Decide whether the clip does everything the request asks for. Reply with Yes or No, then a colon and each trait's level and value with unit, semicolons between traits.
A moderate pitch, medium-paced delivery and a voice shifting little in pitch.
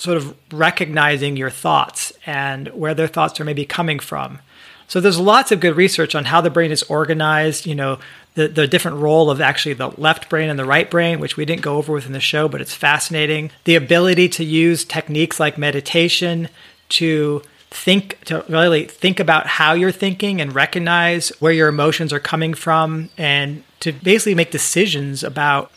Yes: medium, 160 Hz; average, 190 wpm; narrow, 2.3 semitones